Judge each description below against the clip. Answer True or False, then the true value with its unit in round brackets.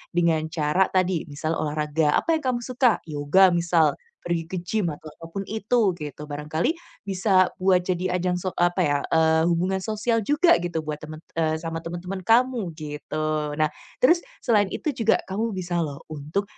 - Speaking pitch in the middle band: True (175 Hz)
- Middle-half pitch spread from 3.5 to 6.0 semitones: True (3.9 semitones)